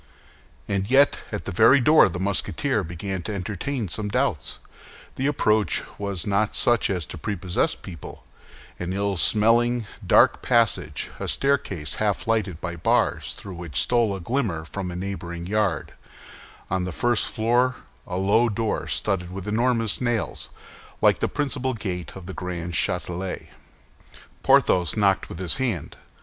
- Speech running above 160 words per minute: No, average, 150 wpm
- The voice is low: Yes, low, 100 Hz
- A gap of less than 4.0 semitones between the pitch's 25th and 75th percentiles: No, average, 4.5 semitones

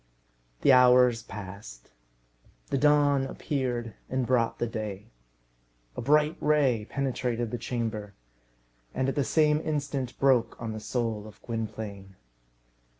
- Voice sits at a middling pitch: No, low, 120 Hz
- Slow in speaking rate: Yes, slow, 125 wpm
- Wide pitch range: No, average, 3.9 semitones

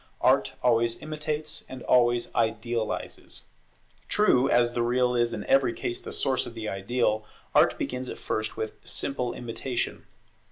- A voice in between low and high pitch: No, low, 120 Hz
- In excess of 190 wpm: No, average, 150 wpm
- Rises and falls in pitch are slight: Yes, narrow, 2.2 semitones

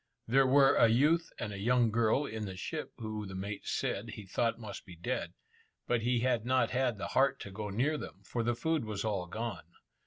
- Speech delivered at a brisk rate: Yes, fast, 220 wpm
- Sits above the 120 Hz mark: No, low, 115 Hz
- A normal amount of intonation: Yes, average, 3.7 semitones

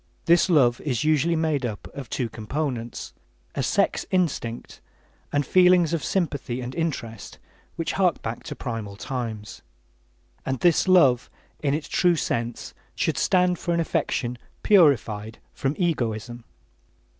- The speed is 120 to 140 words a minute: Yes, slow, 135 wpm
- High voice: No, medium, 140 Hz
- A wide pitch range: Yes, wide, 6.1 semitones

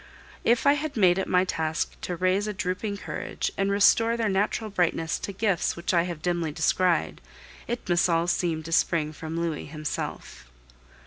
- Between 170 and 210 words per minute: Yes, average, 180 wpm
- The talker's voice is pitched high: No, medium, 180 Hz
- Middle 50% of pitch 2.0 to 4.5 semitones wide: Yes, average, 3.5 semitones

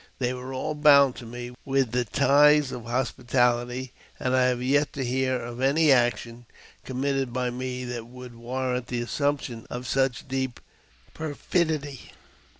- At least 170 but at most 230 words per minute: No, average, 155 wpm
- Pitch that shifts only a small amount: Yes, narrow, 2.0 semitones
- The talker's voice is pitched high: No, low, 130 Hz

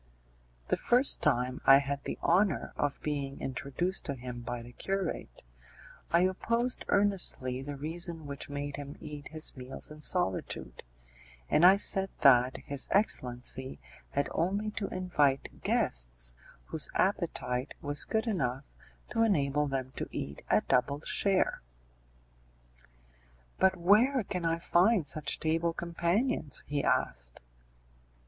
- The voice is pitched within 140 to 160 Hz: Yes, medium, 150 Hz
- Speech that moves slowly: Yes, slow, 130 wpm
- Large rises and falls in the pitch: Yes, wide, 5.7 semitones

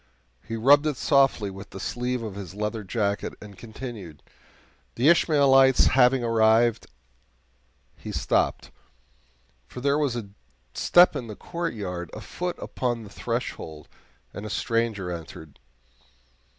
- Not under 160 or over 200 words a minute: No, slow, 135 wpm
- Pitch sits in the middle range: No, low, 115 Hz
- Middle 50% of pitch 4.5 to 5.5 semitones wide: Yes, average, 5.0 semitones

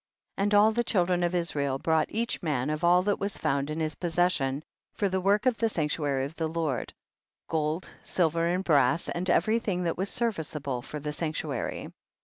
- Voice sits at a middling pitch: Yes, medium, 165 Hz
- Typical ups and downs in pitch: Yes, average, 3.9 semitones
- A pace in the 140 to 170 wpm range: No, average, 195 wpm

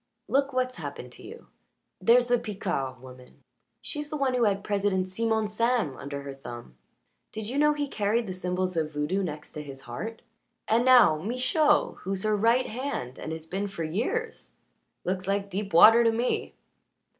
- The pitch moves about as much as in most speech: No, wide, 6.9 semitones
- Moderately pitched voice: No, high, 205 Hz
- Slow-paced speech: No, average, 175 wpm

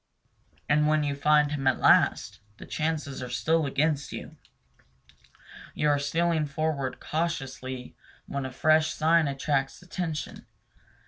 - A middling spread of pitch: No, narrow, 2.2 semitones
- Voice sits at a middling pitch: Yes, medium, 150 Hz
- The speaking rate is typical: No, slow, 130 wpm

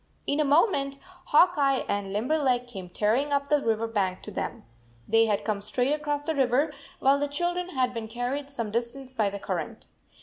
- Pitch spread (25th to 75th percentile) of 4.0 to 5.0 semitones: Yes, average, 4.5 semitones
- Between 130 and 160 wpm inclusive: No, average, 195 wpm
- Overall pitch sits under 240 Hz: No, very high, 260 Hz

